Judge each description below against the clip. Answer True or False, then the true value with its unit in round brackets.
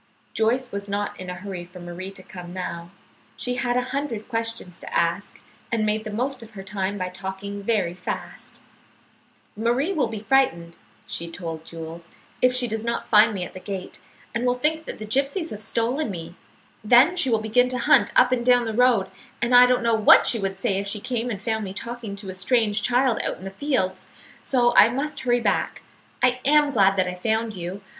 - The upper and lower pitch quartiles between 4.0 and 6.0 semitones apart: True (4.5 semitones)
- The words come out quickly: True (215 wpm)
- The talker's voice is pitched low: False (220 Hz)